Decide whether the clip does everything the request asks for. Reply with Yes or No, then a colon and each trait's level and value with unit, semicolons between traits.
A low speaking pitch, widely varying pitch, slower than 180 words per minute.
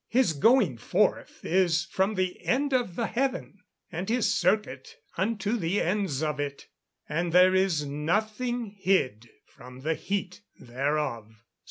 No: medium, 185 Hz; wide, 6.3 semitones; average, 145 wpm